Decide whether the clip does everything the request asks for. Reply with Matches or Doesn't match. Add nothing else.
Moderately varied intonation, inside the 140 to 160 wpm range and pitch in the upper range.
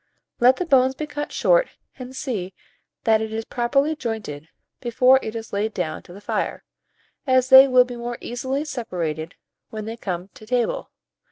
Doesn't match